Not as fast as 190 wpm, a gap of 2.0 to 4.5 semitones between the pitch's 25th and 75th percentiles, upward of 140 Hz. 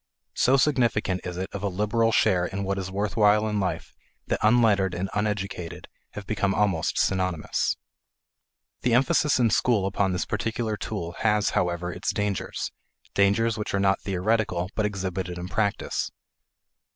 No: average, 155 wpm; average, 2.7 semitones; low, 100 Hz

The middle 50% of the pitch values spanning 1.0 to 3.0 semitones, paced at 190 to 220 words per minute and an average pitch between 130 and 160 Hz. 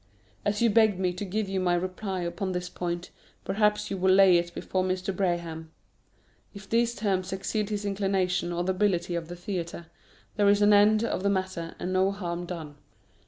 No: narrow, 2.5 semitones; average, 195 wpm; medium, 185 Hz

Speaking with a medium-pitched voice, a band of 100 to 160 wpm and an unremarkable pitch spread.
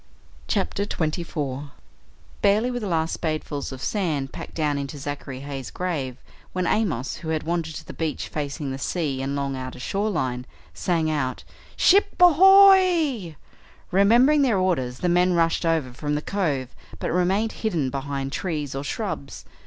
No: medium, 160 Hz; average, 155 wpm; wide, 6.0 semitones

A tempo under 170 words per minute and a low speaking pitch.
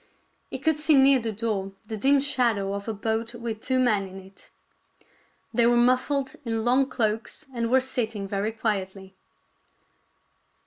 No: average, 160 wpm; high, 230 Hz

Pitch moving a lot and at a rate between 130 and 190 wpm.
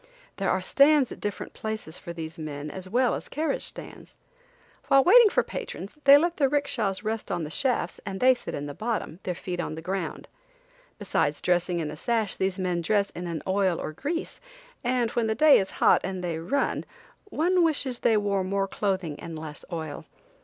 No: wide, 6.9 semitones; average, 200 wpm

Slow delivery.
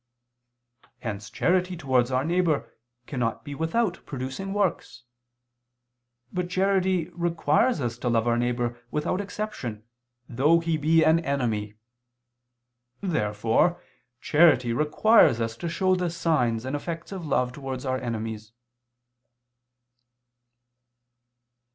Yes: slow, 110 wpm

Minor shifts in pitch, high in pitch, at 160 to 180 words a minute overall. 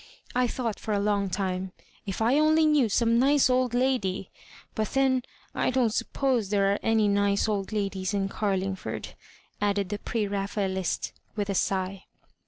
No: average, 3.8 semitones; high, 205 Hz; average, 165 wpm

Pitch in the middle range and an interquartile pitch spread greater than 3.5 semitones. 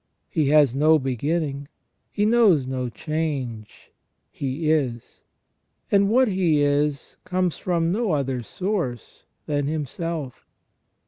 Yes: medium, 150 Hz; average, 4.4 semitones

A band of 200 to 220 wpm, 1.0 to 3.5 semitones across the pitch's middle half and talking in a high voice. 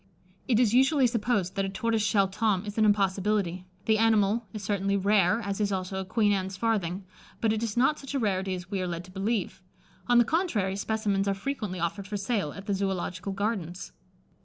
Yes: fast, 205 wpm; average, 2.7 semitones; high, 200 Hz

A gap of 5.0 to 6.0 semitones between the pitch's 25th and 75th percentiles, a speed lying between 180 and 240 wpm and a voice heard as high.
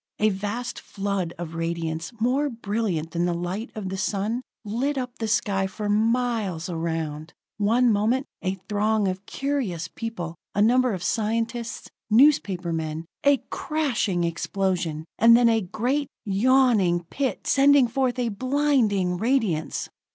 No: wide, 5.5 semitones; average, 140 wpm; high, 210 Hz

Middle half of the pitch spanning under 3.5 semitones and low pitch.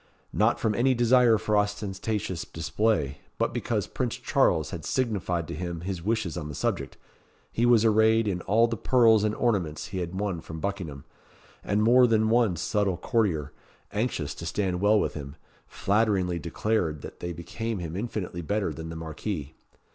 No: average, 4.8 semitones; low, 100 Hz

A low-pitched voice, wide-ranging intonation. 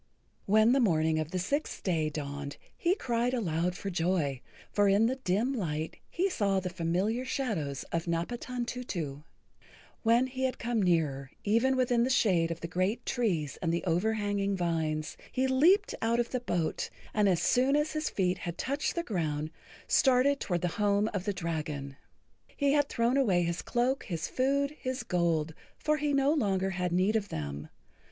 No: high, 200 Hz; wide, 7.0 semitones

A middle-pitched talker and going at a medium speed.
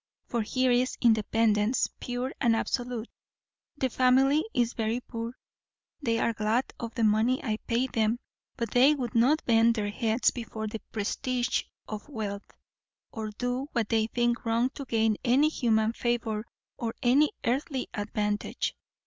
No: high, 235 Hz; average, 150 wpm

